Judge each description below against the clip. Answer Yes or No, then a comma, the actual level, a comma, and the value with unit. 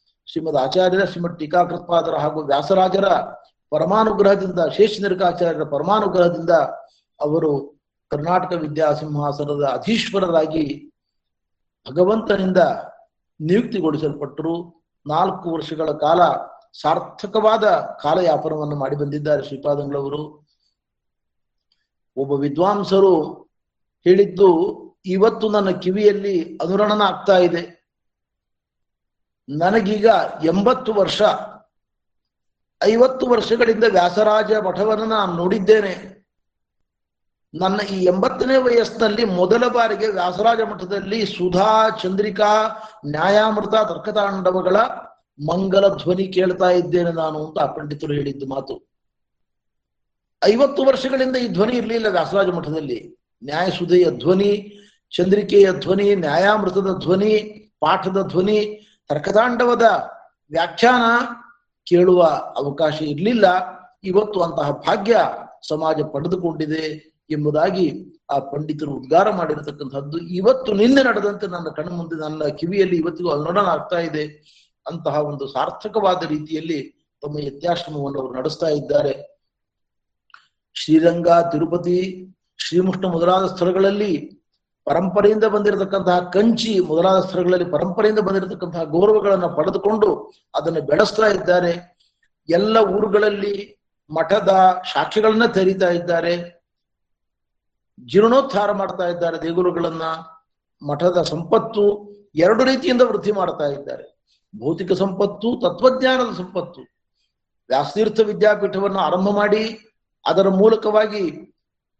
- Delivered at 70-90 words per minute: Yes, average, 85 wpm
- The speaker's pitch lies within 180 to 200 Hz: Yes, medium, 185 Hz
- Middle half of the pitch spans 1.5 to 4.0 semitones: No, average, 4.6 semitones